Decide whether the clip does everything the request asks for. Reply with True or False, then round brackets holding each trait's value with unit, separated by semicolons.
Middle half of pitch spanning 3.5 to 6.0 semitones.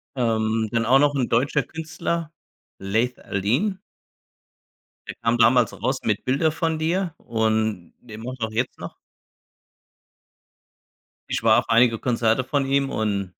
True (3.9 semitones)